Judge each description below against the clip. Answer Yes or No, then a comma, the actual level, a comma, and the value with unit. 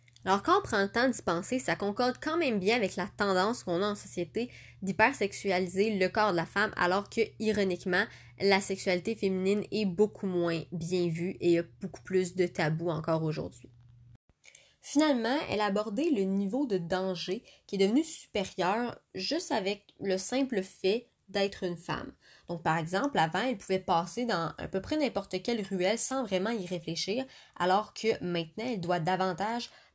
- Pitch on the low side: No, high, 195 Hz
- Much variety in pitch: No, average, 3.6 semitones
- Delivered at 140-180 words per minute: Yes, average, 175 wpm